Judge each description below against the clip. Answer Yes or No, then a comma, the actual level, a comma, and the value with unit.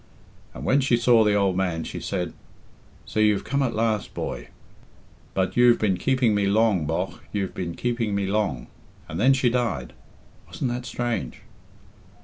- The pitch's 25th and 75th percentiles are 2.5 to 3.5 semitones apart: No, average, 4.2 semitones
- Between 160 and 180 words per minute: Yes, average, 165 wpm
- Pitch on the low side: Yes, low, 105 Hz